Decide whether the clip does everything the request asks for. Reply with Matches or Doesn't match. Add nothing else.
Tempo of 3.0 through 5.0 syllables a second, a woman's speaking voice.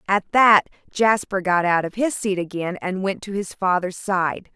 Matches